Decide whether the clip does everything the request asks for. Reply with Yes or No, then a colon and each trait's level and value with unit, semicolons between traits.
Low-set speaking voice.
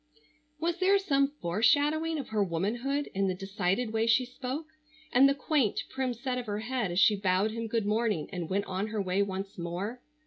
No: high, 220 Hz